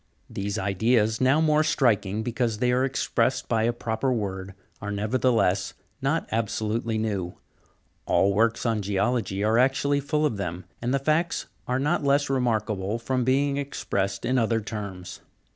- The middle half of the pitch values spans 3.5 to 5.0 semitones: Yes, average, 4.2 semitones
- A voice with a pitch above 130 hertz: No, low, 115 Hz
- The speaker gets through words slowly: No, average, 155 wpm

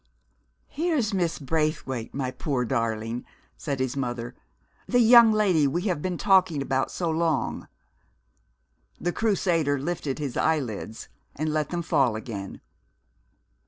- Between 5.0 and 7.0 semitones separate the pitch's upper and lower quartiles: Yes, average, 5.3 semitones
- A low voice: No, medium, 150 Hz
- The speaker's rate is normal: No, slow, 125 wpm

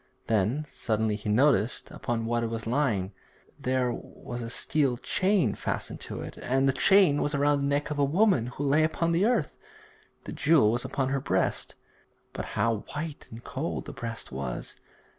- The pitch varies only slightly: No, average, 4.4 semitones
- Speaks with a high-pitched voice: No, low, 130 Hz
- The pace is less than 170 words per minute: No, average, 180 wpm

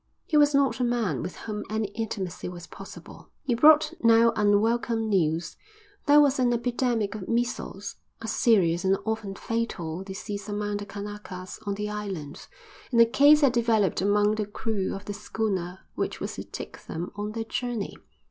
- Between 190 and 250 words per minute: No, average, 175 wpm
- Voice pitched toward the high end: Yes, high, 210 Hz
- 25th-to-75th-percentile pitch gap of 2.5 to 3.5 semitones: Yes, average, 3.1 semitones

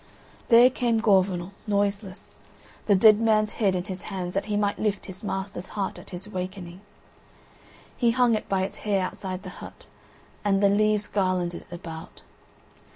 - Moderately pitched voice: No, high, 200 Hz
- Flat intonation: Yes, narrow, 2.3 semitones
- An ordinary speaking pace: Yes, average, 165 wpm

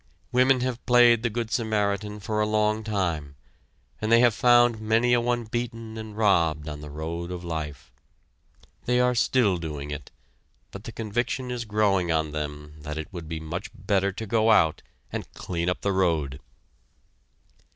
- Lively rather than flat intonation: Yes, wide, 6.2 semitones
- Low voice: Yes, low, 105 Hz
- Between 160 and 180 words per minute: Yes, average, 170 wpm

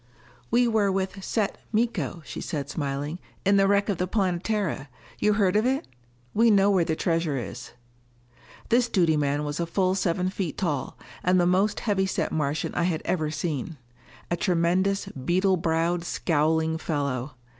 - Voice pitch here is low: No, medium, 175 Hz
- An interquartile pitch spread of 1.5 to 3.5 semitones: No, average, 4.0 semitones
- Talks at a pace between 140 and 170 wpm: Yes, average, 165 wpm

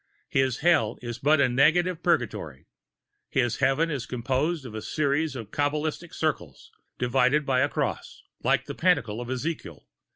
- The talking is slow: No, average, 155 wpm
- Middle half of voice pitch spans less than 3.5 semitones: No, average, 4.2 semitones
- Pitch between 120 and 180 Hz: Yes, low, 135 Hz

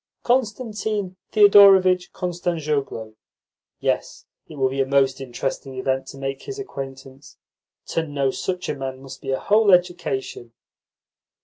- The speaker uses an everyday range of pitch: No, wide, 5.9 semitones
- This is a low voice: No, medium, 145 Hz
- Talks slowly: Yes, slow, 130 wpm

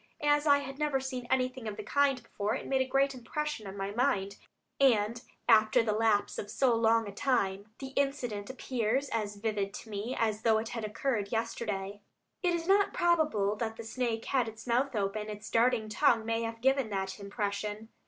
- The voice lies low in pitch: No, high, 230 Hz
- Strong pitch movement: No, average, 4.0 semitones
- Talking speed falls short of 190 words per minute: No, average, 195 wpm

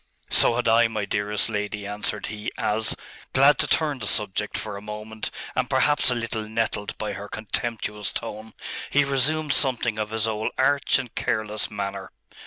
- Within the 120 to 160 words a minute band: No, average, 175 wpm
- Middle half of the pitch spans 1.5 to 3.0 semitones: Yes, narrow, 2.4 semitones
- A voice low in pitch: Yes, low, 110 Hz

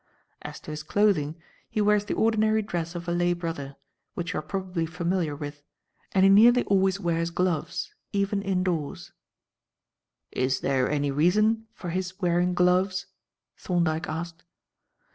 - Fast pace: No, average, 145 wpm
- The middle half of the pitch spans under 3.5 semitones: Yes, average, 3.1 semitones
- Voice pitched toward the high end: No, medium, 175 Hz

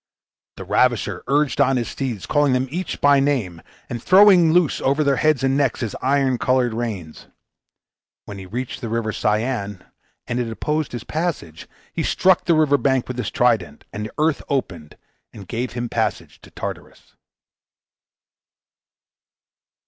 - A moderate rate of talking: Yes, average, 160 wpm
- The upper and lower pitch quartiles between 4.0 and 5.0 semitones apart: Yes, average, 4.7 semitones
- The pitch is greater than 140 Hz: No, low, 125 Hz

